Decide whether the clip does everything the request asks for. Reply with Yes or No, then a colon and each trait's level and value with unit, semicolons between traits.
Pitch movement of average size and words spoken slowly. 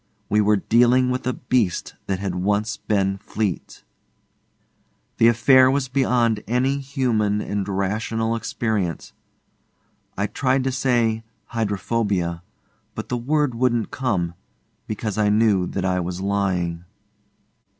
Yes: average, 4.0 semitones; slow, 125 wpm